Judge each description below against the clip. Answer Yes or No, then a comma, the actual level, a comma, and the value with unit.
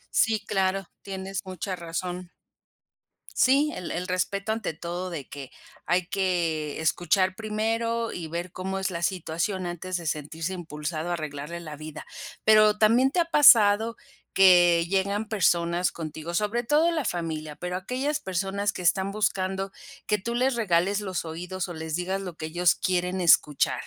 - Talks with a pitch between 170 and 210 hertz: Yes, medium, 185 Hz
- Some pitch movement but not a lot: Yes, average, 3.4 semitones